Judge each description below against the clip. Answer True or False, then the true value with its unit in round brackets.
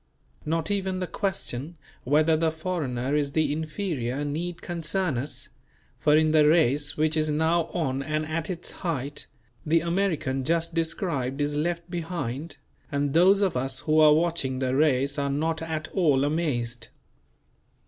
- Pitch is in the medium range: True (155 Hz)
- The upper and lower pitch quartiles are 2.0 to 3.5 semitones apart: True (3.0 semitones)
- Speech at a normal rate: True (155 wpm)